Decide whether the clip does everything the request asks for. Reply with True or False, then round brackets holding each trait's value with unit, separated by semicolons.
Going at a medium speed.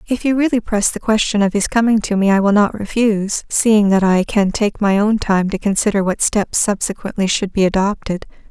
False (220 wpm)